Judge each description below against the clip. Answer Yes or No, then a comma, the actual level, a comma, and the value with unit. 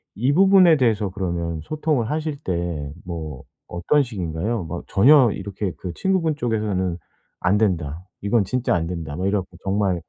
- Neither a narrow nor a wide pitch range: No, wide, 6.5 semitones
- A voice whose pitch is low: Yes, low, 100 Hz